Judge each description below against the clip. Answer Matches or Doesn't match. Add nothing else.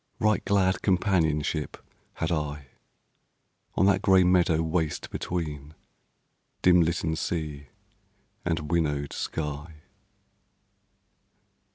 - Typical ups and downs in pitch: Matches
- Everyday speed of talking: Doesn't match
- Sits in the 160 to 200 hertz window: Doesn't match